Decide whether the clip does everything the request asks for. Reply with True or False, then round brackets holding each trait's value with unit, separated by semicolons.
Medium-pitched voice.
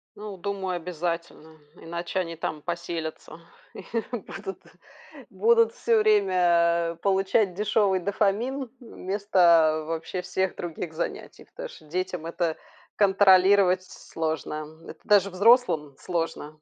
True (180 Hz)